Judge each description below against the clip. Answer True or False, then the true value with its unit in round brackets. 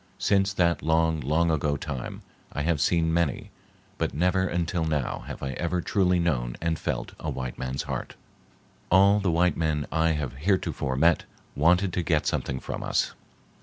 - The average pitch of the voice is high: False (80 Hz)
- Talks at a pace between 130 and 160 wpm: False (170 wpm)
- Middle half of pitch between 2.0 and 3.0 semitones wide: False (3.4 semitones)